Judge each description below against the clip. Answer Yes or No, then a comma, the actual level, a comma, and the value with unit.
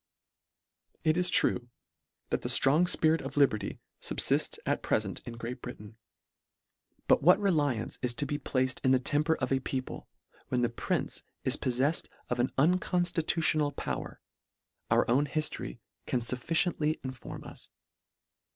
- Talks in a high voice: No, medium, 140 Hz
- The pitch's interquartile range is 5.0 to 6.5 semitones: No, average, 4.1 semitones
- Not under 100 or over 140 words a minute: No, average, 150 wpm